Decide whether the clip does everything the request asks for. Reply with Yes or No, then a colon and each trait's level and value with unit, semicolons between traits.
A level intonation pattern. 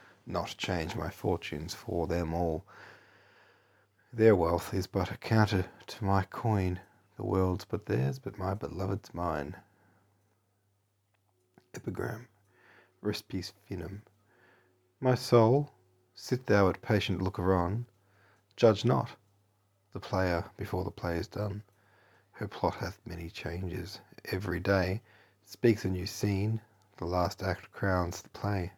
Yes: narrow, 2.2 semitones